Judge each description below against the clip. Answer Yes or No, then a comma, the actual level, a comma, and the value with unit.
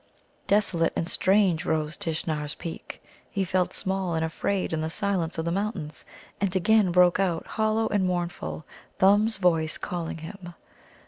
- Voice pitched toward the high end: No, medium, 180 Hz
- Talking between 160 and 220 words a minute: No, average, 150 wpm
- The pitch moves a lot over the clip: No, average, 3.3 semitones